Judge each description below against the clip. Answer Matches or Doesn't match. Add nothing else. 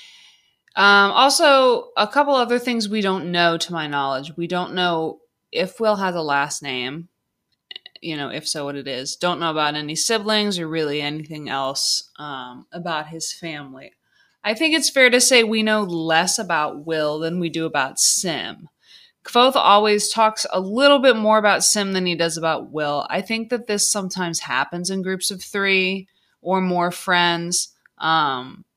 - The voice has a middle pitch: Matches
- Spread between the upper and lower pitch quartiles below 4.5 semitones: Doesn't match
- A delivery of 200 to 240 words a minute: Doesn't match